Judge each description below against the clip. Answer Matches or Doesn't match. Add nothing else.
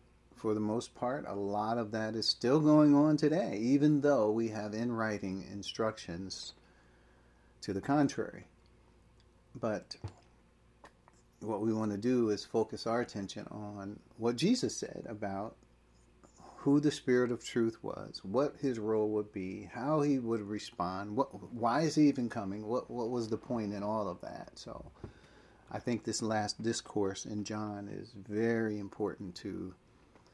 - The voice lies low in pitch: Matches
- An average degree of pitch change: Matches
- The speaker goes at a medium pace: Matches